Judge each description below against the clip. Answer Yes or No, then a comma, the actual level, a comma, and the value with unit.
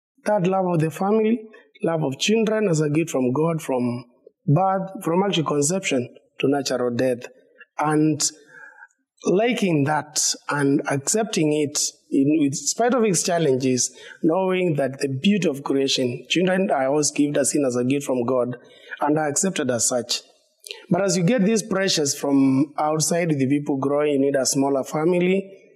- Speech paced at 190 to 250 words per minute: No, average, 160 wpm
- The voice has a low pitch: No, medium, 155 Hz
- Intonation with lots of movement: Yes, wide, 5.8 semitones